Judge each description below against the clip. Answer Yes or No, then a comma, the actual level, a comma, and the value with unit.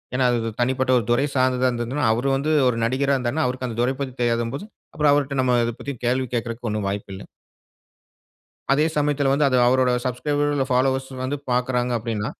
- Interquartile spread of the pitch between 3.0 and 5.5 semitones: No, narrow, 2.5 semitones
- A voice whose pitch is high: No, low, 130 Hz